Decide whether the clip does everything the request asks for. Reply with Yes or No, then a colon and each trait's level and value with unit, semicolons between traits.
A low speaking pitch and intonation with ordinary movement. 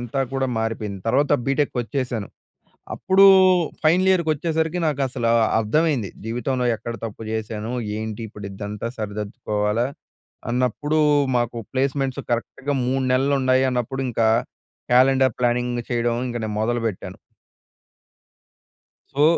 Yes: low, 125 Hz; average, 3.4 semitones